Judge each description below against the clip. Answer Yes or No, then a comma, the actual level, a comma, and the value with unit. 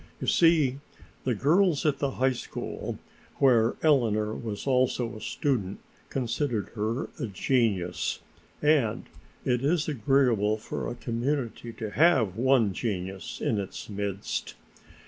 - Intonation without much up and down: No, average, 4.4 semitones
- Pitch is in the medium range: No, low, 120 Hz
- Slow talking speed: Yes, slow, 125 wpm